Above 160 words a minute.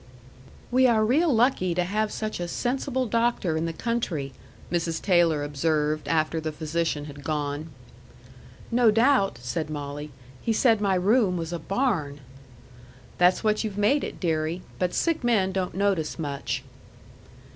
No: average, 150 wpm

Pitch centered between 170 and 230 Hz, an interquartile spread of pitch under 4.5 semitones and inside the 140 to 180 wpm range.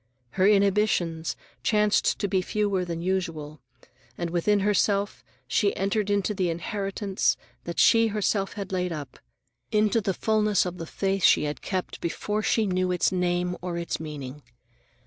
Yes: high, 190 Hz; average, 3.1 semitones; average, 155 wpm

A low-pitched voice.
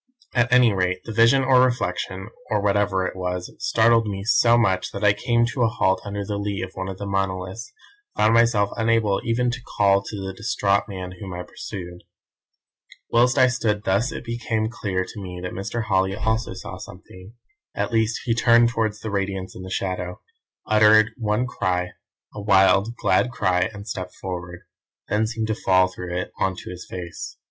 Yes: low, 100 Hz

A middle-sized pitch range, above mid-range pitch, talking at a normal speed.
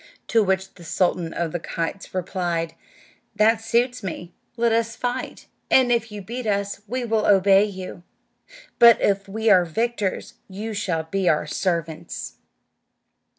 Yes: average, 4.2 semitones; high, 200 Hz; average, 150 wpm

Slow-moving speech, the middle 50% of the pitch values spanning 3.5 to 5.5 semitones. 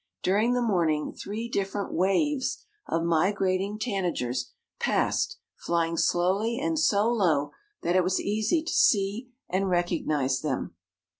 Yes: slow, 130 wpm; average, 4.4 semitones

